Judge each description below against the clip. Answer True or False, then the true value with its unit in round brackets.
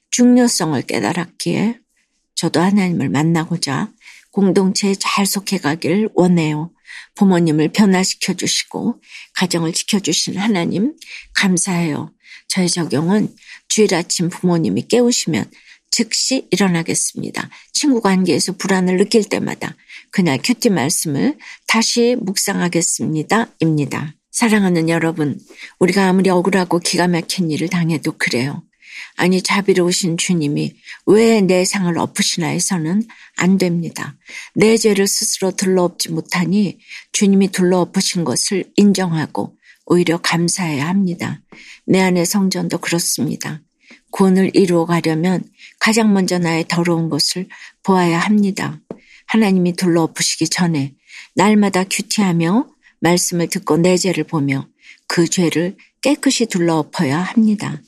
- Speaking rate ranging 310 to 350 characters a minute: False (295 characters per minute)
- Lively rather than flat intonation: False (3.3 semitones)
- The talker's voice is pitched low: False (180 Hz)